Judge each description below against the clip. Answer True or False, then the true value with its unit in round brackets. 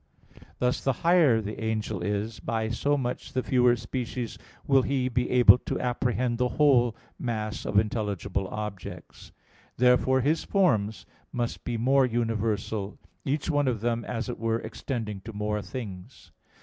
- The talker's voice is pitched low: True (120 Hz)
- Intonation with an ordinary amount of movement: True (3.0 semitones)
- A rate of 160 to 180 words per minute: False (150 wpm)